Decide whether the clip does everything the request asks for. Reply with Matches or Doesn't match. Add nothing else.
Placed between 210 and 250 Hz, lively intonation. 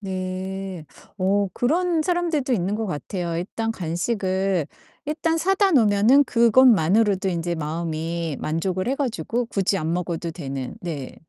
Doesn't match